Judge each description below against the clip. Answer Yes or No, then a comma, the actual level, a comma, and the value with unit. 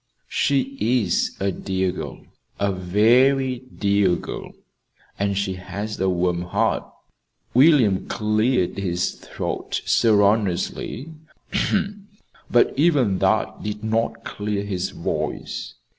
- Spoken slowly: Yes, slow, 105 wpm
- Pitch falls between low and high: No, low, 105 Hz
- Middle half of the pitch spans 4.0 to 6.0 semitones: Yes, average, 4.3 semitones